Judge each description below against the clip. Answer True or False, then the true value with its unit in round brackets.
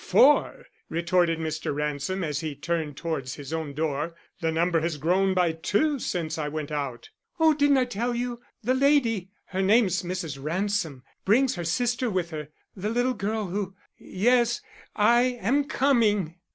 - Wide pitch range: True (6.9 semitones)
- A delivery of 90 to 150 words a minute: False (165 wpm)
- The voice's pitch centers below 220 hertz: True (185 Hz)